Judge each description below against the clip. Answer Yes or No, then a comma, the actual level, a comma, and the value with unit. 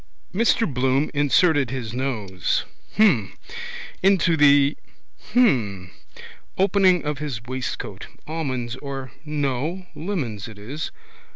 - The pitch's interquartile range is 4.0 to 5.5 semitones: Yes, average, 5.0 semitones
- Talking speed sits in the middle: No, slow, 100 wpm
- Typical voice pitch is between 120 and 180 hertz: Yes, medium, 140 Hz